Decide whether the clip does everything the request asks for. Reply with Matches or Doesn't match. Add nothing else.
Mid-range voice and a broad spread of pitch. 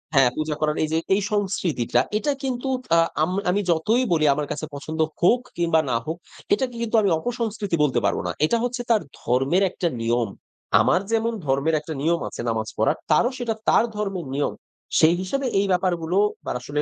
Matches